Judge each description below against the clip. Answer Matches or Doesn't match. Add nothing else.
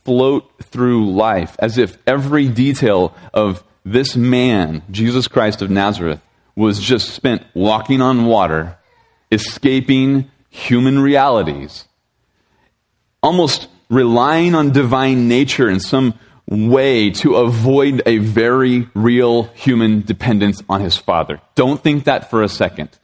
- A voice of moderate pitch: Doesn't match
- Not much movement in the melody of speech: Doesn't match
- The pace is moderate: Doesn't match